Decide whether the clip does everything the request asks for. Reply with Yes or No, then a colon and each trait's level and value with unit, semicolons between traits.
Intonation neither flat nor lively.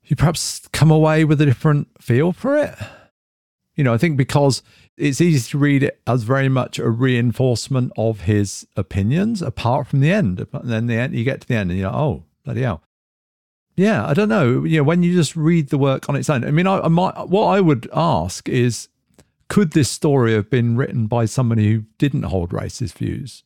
Yes: average, 5.0 semitones